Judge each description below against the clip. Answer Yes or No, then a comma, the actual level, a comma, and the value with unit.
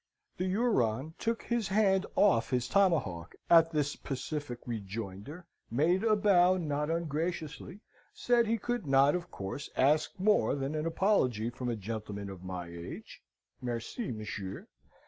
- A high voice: No, medium, 150 Hz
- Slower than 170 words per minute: Yes, average, 145 wpm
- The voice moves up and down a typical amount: No, wide, 8.4 semitones